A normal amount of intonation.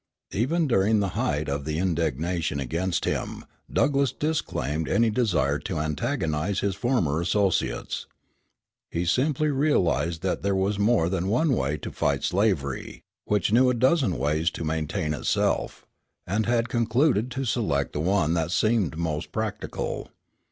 No: wide, 6.9 semitones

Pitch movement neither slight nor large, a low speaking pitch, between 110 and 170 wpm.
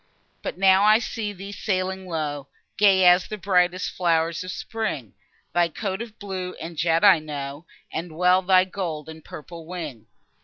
No: average, 3.0 semitones; medium, 180 Hz; average, 165 wpm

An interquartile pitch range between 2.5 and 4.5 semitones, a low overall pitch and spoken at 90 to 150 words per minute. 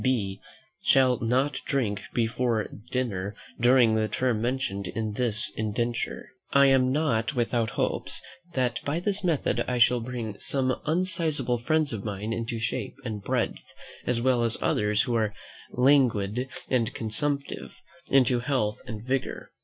Yes: average, 3.2 semitones; low, 120 Hz; average, 145 wpm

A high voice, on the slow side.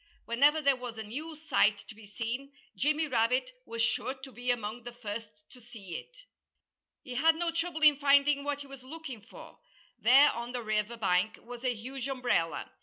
No: very high, 250 Hz; average, 190 wpm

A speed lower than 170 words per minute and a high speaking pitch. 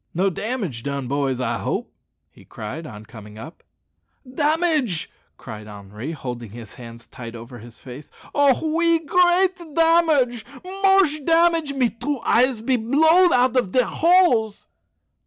Yes: average, 140 wpm; high, 235 Hz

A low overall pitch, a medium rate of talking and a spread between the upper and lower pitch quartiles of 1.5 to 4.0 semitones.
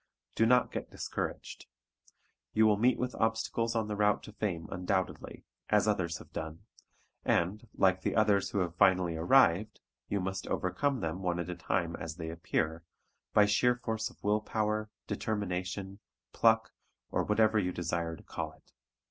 Yes: low, 100 Hz; average, 165 wpm; average, 3.5 semitones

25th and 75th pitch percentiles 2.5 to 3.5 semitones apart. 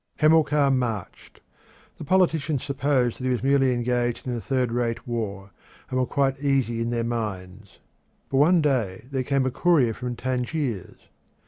Yes: average, 3.0 semitones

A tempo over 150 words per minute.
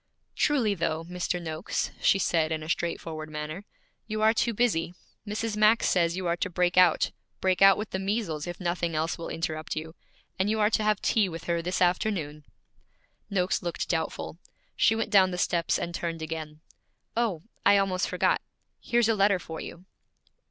Yes: average, 185 wpm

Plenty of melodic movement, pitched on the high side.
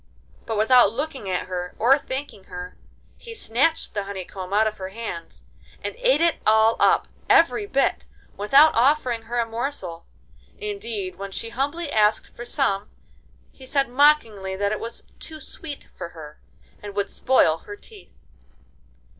Yes: wide, 6.4 semitones; high, 230 Hz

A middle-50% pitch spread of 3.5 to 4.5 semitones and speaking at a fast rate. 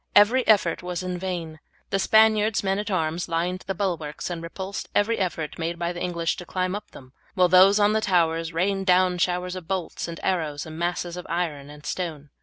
No: narrow, 2.5 semitones; fast, 210 wpm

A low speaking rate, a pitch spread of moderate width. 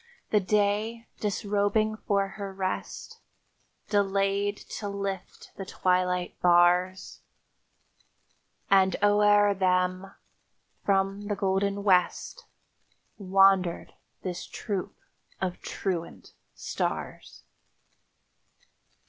No: slow, 80 wpm; narrow, 1.6 semitones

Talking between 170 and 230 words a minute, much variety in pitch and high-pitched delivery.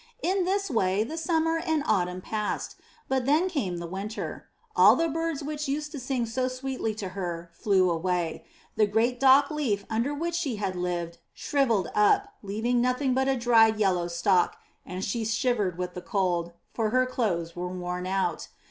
Yes: average, 180 wpm; wide, 6.7 semitones; high, 220 Hz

